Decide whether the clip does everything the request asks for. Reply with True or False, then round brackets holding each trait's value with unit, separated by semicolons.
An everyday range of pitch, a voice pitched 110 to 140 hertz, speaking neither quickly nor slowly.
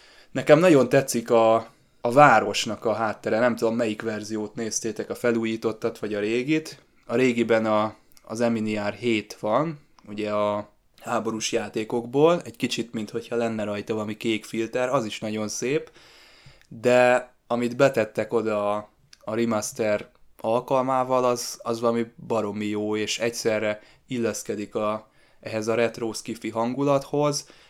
False (2.3 semitones; 115 Hz; 135 wpm)